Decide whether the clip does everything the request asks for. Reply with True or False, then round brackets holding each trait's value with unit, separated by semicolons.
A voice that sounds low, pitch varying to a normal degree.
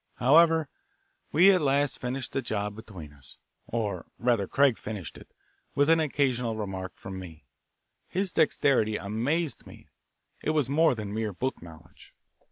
False (120 Hz; 6.1 semitones)